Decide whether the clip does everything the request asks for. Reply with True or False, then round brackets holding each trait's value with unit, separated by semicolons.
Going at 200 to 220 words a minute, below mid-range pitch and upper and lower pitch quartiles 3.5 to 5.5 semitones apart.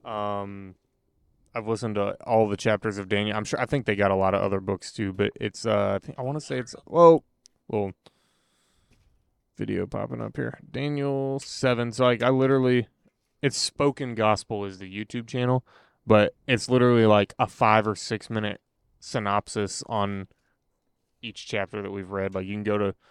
False (185 wpm; 110 Hz; 3.8 semitones)